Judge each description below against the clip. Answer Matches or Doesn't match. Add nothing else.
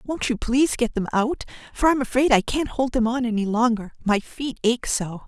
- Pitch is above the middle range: Matches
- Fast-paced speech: Matches